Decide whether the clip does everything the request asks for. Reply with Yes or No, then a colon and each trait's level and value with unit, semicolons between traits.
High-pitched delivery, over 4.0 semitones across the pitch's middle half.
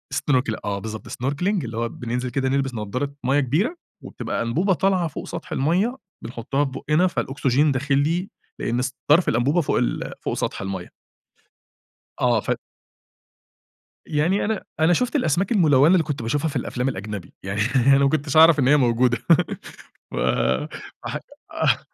No: medium, 140 Hz; average, 4.9 semitones